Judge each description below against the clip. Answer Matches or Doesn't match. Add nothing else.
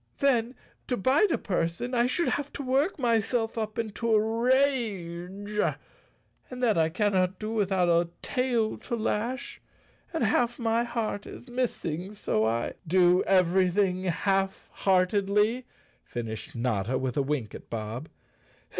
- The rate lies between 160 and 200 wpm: Doesn't match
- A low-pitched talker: Doesn't match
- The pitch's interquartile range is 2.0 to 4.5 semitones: Doesn't match